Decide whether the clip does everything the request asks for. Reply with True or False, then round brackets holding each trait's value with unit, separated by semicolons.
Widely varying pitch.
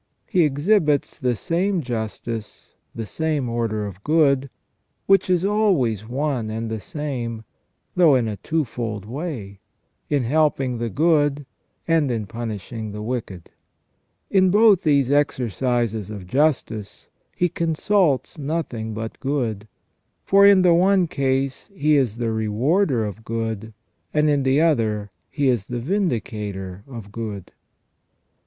True (5.9 semitones)